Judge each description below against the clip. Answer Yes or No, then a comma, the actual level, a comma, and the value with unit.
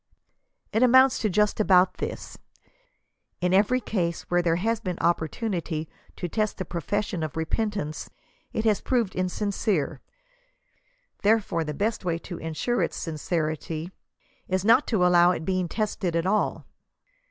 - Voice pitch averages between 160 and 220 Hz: Yes, medium, 185 Hz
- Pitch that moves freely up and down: No, average, 4.2 semitones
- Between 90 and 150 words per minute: Yes, average, 140 wpm